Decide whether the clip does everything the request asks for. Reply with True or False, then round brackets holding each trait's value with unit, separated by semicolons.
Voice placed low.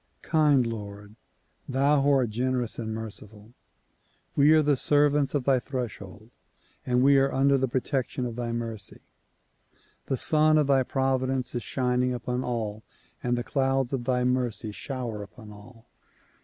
True (125 Hz)